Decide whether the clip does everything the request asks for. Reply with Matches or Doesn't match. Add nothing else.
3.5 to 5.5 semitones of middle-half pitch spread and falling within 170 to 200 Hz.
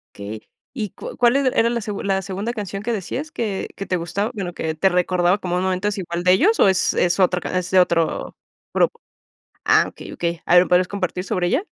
Doesn't match